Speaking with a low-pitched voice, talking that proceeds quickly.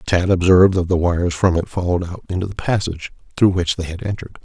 Yes: very low, 90 Hz; fast, 230 wpm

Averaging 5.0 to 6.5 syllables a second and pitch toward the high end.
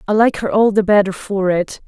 Yes: 5.4 syllables/s; high, 200 Hz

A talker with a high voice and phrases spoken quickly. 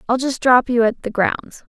Yes: high, 240 Hz; fast, 240 wpm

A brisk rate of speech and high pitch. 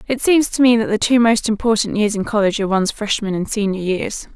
Yes: fast, 250 wpm; high, 215 Hz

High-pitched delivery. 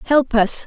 Yes: very high, 250 Hz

